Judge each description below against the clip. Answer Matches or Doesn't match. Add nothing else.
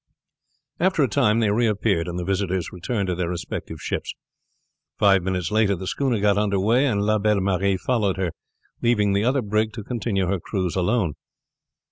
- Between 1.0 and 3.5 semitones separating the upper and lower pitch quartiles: Matches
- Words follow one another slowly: Doesn't match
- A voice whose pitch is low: Matches